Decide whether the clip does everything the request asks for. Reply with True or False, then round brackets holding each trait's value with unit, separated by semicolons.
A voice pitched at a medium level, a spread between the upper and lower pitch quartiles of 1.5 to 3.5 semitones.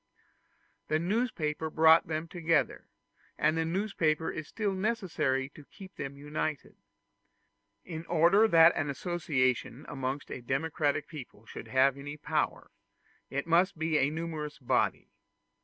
True (155 Hz; 2.9 semitones)